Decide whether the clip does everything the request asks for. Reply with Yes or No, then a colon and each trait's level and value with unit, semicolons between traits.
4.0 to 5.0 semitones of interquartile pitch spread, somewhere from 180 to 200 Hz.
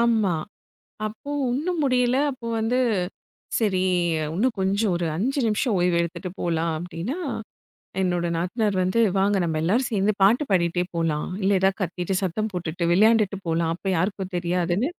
Yes: average, 4.3 semitones; high, 190 Hz